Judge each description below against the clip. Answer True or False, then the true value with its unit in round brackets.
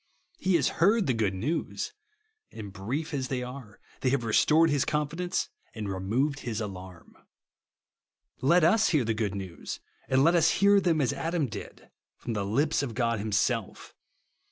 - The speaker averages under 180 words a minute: True (170 wpm)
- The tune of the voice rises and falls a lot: True (6.8 semitones)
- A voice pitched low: True (130 Hz)